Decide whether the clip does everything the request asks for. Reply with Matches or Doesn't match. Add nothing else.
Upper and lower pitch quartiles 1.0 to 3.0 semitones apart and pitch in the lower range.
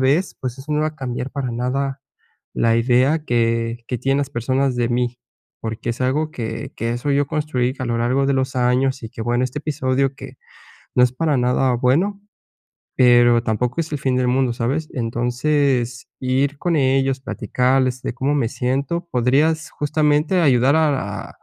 Matches